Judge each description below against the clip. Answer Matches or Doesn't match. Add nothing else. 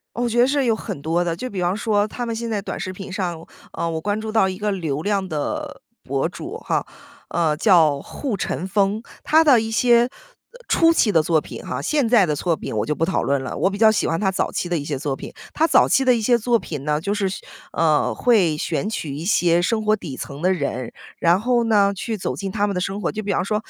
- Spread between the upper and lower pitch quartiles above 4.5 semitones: Matches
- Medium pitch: Doesn't match